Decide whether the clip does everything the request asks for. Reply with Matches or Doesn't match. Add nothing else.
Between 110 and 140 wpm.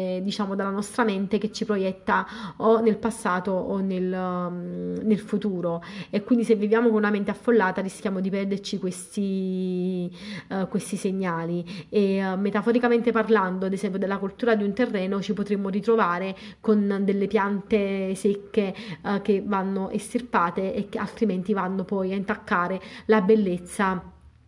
Doesn't match